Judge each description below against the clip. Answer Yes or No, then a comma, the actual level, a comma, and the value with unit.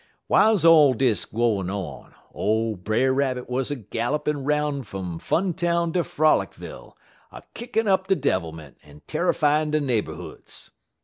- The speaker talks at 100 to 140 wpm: Yes, slow, 135 wpm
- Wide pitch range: Yes, wide, 6.5 semitones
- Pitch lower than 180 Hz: Yes, low, 135 Hz